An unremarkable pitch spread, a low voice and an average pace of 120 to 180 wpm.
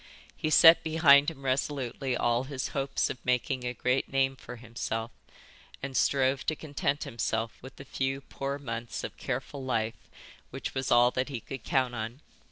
No: narrow, 2.2 semitones; low, 130 Hz; average, 175 wpm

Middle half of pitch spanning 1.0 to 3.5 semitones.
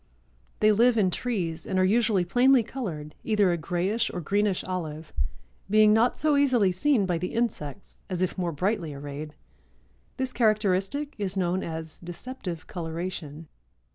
No: average, 4.8 semitones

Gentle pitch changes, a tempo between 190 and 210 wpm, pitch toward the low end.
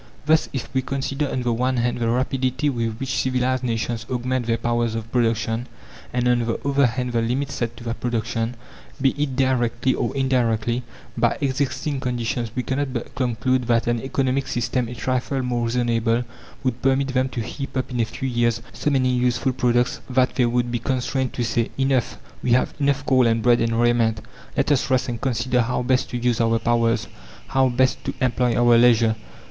Yes: narrow, 1.9 semitones; average, 195 wpm; low, 125 Hz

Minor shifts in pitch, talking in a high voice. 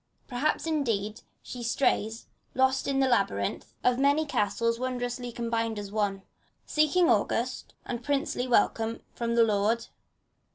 No: average, 3.2 semitones; high, 235 Hz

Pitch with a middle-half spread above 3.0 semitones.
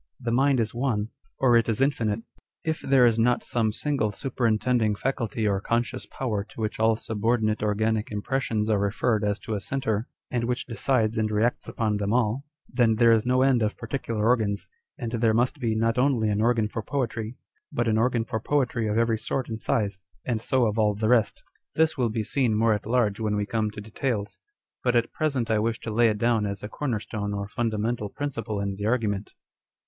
No: narrow, 2.5 semitones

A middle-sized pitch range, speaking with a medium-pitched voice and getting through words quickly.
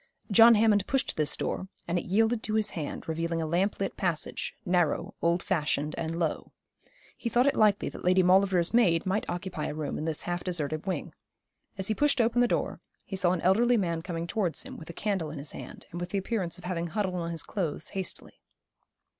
Yes: average, 3.7 semitones; medium, 180 Hz; fast, 215 wpm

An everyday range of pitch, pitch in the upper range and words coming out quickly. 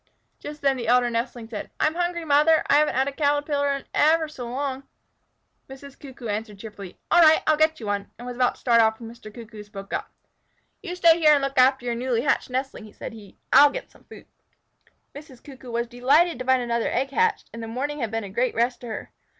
Yes: average, 3.9 semitones; very high, 255 Hz; fast, 230 wpm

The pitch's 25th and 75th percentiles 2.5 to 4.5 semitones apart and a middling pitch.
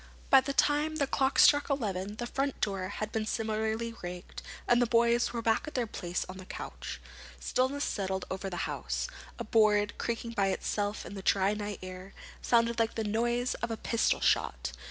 No: average, 3.4 semitones; high, 220 Hz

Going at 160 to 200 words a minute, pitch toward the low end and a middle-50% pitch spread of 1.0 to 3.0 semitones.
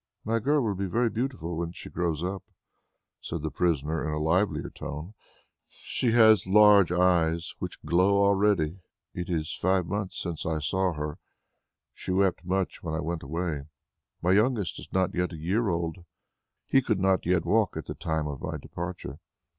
No: average, 180 wpm; very low, 90 Hz; average, 3.5 semitones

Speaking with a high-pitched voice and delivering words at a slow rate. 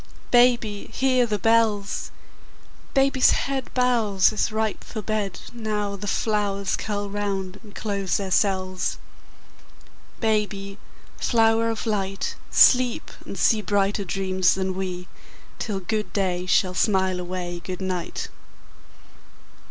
Yes: high, 205 Hz; slow, 120 wpm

